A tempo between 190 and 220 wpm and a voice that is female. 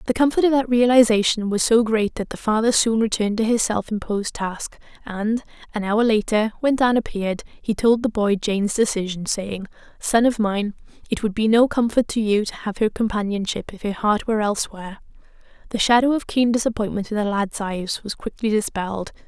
Yes: average, 195 wpm; female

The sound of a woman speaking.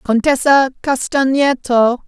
Yes: female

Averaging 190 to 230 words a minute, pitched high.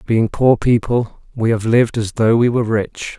No: fast, 205 wpm; low, 115 Hz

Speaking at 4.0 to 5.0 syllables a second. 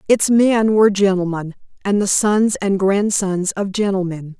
Yes: 4.3 syllables/s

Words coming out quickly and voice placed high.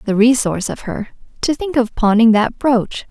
No: average, 195 wpm; high, 235 Hz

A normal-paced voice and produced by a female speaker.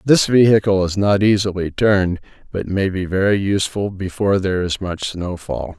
No: average, 165 wpm; male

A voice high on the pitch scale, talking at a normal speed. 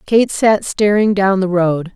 Yes: high, 195 Hz; average, 185 wpm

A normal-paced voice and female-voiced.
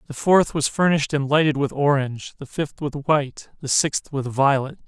No: average, 170 wpm; male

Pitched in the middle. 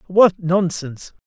Yes: medium, 175 Hz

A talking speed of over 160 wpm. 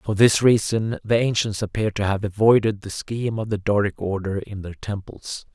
Yes: average, 195 wpm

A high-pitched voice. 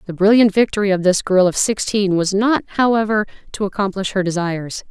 Yes: high, 200 Hz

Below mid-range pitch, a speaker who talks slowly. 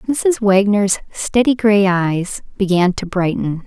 No: high, 200 Hz; slow, 130 wpm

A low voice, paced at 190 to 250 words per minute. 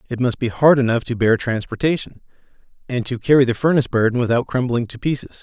Yes: low, 125 Hz; average, 200 wpm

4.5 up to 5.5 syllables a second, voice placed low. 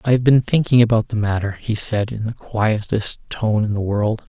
Yes: 4.9 syllables/s; low, 110 Hz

